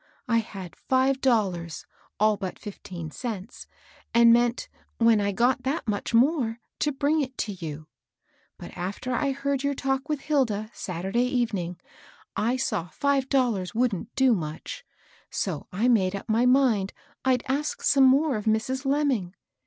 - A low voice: No, high, 235 Hz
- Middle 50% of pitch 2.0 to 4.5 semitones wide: No, average, 5.0 semitones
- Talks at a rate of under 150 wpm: No, average, 155 wpm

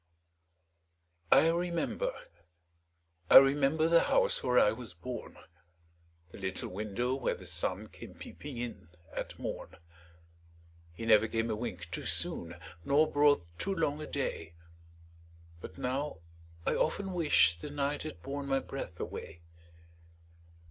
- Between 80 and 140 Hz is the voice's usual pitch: Yes, low, 135 Hz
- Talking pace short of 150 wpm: Yes, slow, 135 wpm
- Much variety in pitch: Yes, wide, 6.2 semitones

